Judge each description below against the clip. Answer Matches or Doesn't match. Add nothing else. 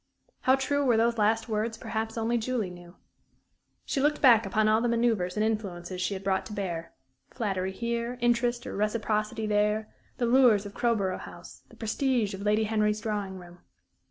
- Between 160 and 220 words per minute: Matches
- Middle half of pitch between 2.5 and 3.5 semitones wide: Matches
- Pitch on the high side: Matches